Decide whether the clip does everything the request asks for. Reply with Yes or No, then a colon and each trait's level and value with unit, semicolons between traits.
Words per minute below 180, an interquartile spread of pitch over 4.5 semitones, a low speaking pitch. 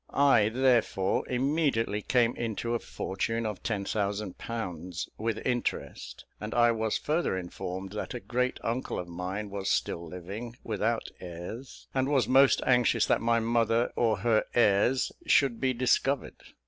No: average, 150 wpm; average, 3.7 semitones; low, 115 Hz